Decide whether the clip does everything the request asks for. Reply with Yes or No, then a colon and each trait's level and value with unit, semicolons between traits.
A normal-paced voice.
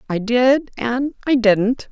Yes: average, 155 wpm